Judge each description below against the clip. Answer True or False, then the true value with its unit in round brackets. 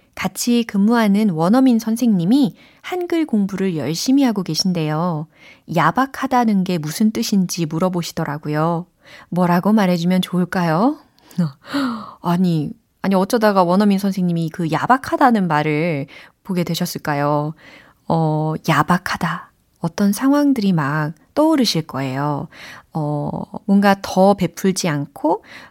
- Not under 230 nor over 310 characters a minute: True (270 characters per minute)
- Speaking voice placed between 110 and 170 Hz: False (185 Hz)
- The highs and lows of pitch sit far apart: False (5.0 semitones)